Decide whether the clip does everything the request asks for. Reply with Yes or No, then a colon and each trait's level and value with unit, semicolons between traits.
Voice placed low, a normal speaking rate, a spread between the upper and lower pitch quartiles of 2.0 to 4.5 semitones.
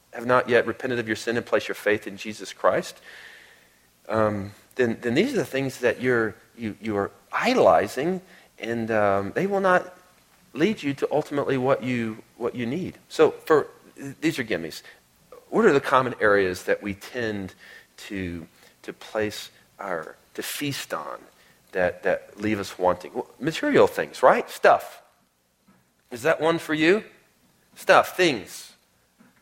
No: low, 115 Hz; average, 160 wpm; average, 5.3 semitones